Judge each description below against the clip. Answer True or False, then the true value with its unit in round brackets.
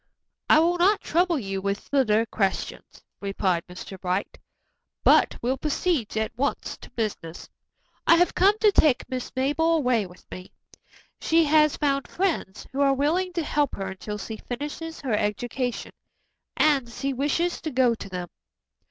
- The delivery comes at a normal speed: True (160 wpm)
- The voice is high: True (265 Hz)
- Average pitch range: False (7.0 semitones)